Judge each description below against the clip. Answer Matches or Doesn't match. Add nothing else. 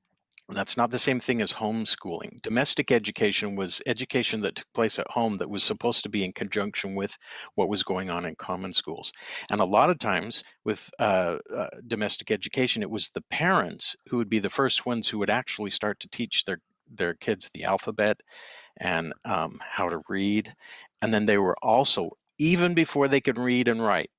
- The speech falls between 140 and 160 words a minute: Doesn't match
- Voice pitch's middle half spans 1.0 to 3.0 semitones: Doesn't match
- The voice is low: Matches